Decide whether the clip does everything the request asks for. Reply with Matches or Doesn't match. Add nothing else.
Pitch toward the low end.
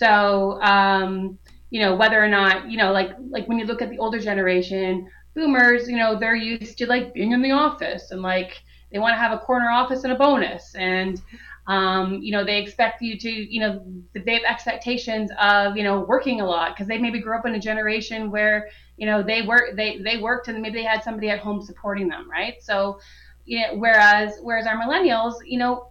Doesn't match